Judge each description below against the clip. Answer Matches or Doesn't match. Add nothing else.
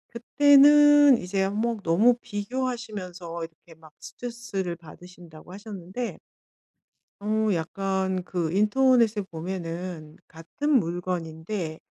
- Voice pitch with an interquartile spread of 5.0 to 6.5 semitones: Matches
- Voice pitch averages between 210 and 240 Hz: Doesn't match